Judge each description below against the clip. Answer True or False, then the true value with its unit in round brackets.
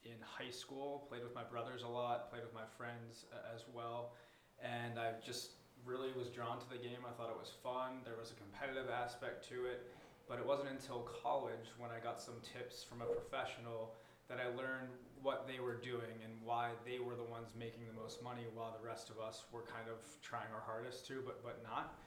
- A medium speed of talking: False (225 wpm)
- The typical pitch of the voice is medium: False (120 Hz)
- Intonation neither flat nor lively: False (1.4 semitones)